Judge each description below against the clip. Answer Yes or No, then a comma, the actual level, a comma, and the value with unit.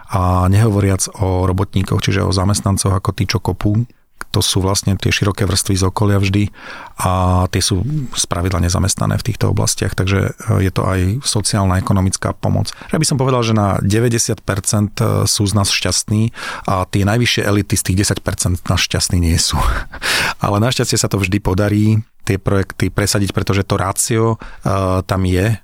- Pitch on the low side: Yes, low, 100 Hz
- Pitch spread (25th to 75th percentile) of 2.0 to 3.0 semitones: Yes, average, 2.7 semitones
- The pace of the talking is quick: Yes, fast, 170 wpm